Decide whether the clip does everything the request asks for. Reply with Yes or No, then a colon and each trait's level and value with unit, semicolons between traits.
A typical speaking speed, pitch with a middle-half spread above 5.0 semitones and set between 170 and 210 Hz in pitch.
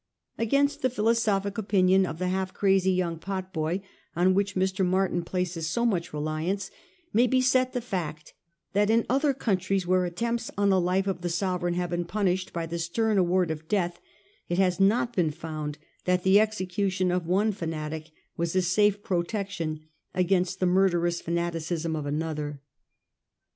No: average, 175 wpm; average, 2.7 semitones; medium, 185 Hz